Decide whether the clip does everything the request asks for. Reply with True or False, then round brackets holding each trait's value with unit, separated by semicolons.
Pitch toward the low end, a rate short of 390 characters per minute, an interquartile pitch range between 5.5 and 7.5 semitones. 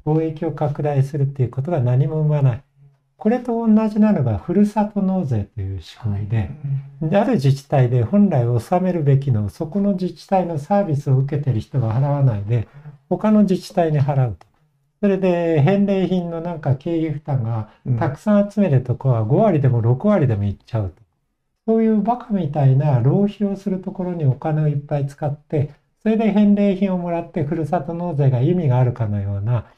False (150 Hz; 365 characters per minute; 5.9 semitones)